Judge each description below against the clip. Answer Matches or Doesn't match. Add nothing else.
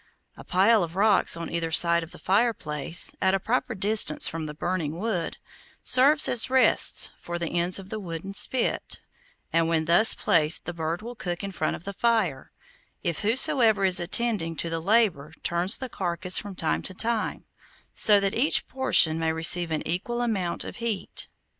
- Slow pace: Doesn't match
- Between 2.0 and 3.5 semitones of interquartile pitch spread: Doesn't match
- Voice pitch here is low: Doesn't match